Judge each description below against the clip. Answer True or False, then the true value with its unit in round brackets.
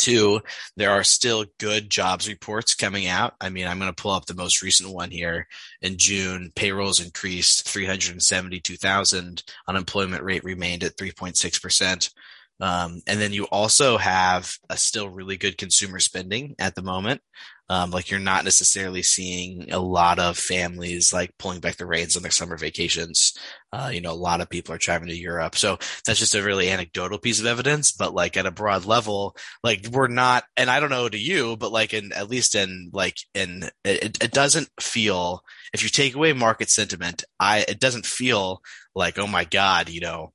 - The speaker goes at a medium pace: True (190 wpm)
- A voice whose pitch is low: True (95 Hz)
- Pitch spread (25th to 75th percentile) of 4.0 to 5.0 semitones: False (3.1 semitones)